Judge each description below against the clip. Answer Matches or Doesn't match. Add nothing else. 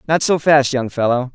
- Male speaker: Matches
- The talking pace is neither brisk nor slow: Doesn't match